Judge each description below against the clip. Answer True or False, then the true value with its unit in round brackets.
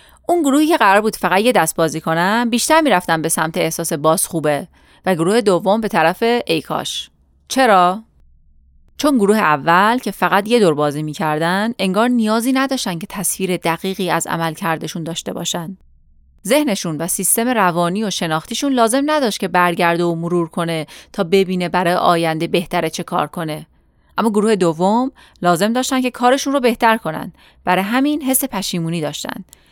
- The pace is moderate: False (160 wpm)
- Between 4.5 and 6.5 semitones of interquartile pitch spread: True (5.6 semitones)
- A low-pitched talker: False (185 Hz)